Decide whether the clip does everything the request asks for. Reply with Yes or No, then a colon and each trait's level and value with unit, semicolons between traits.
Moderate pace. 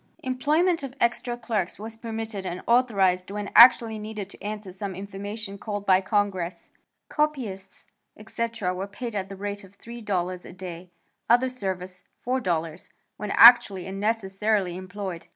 Yes: average, 150 wpm